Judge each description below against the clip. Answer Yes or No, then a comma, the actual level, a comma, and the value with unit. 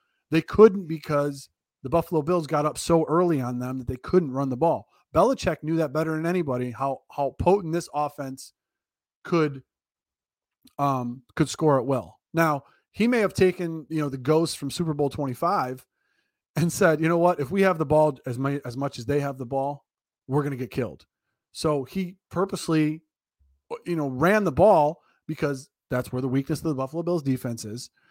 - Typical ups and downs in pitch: Yes, average, 4.0 semitones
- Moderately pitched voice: Yes, medium, 150 Hz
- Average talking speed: Yes, average, 195 wpm